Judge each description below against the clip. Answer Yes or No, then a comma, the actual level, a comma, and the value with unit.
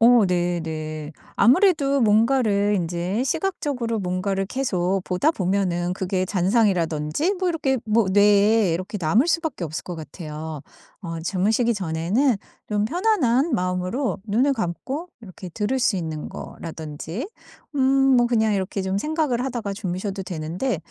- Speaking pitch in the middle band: No, high, 200 Hz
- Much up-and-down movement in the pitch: Yes, wide, 5.9 semitones